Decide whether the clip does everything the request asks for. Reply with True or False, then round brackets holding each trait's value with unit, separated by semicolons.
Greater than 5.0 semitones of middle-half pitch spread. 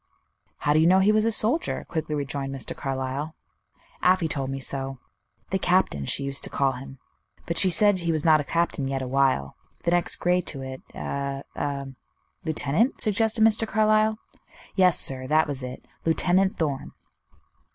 True (5.4 semitones)